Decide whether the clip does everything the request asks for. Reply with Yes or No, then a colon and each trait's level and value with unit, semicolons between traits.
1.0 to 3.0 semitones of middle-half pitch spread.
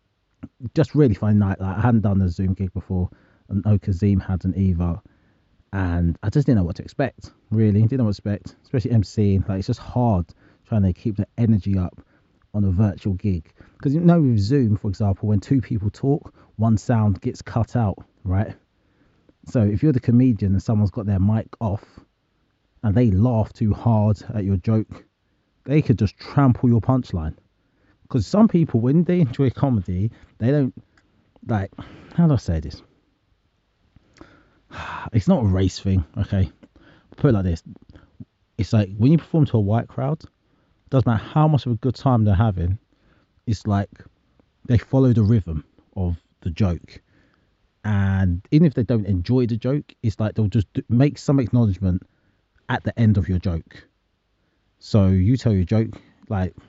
No: average, 3.9 semitones